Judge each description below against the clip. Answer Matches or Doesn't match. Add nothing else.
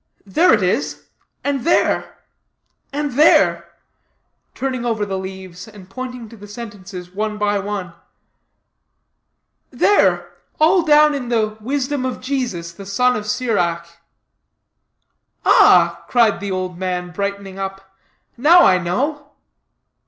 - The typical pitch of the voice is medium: Doesn't match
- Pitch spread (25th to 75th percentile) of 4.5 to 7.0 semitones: Matches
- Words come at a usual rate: Doesn't match